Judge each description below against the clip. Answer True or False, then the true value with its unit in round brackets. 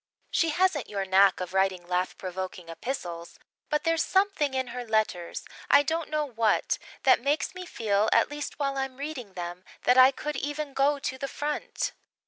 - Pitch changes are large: True (7.5 semitones)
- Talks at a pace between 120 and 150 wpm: False (180 wpm)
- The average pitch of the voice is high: True (260 Hz)